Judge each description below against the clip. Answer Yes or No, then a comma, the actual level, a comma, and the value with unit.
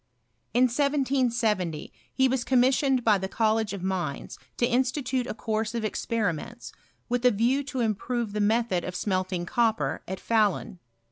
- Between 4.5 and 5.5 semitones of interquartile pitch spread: No, average, 3.7 semitones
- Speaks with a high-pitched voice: Yes, high, 230 Hz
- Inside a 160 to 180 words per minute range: No, average, 150 wpm